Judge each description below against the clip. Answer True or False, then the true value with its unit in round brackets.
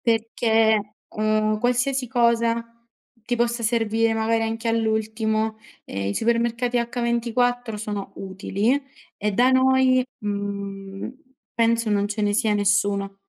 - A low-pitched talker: False (225 Hz)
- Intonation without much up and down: True (2.2 semitones)